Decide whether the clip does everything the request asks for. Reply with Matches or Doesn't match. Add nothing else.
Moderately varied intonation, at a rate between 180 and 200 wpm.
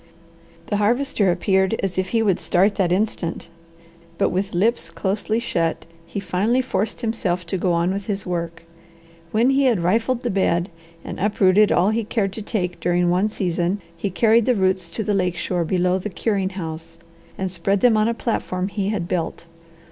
Matches